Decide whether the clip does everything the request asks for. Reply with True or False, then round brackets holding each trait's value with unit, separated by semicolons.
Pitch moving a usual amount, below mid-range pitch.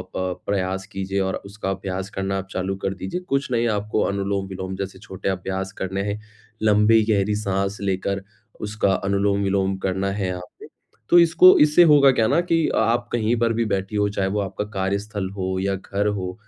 False (1.8 semitones; 100 Hz)